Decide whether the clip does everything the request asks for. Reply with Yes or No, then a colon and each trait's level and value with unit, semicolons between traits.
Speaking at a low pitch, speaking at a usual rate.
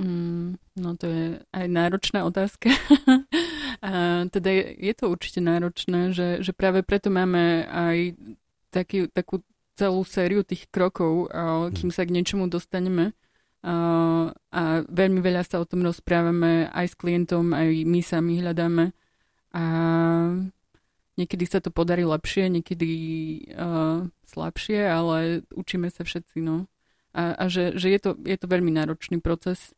No: medium, 175 Hz; average, 140 wpm